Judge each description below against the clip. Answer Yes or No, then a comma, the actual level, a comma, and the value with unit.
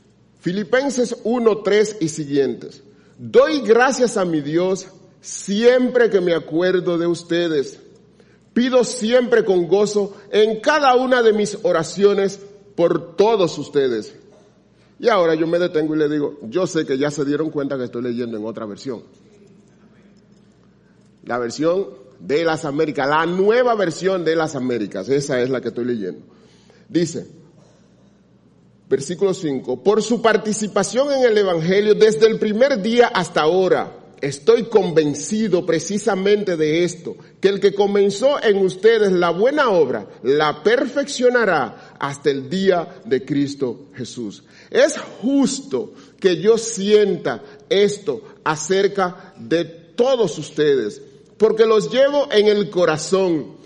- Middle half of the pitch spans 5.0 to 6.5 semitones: Yes, wide, 5.6 semitones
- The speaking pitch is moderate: No, high, 195 Hz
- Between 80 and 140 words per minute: Yes, average, 135 wpm